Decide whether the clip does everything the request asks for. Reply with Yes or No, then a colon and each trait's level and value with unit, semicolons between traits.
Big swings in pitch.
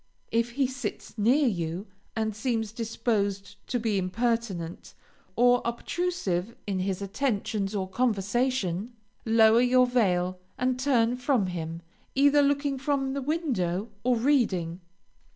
No: average, 4.6 semitones